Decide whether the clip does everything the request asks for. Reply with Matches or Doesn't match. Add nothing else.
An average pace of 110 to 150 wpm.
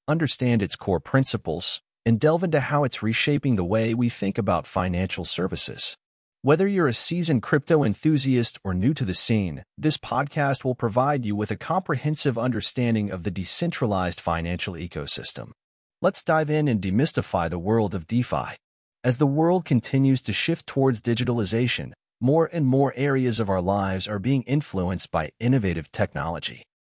Doesn't match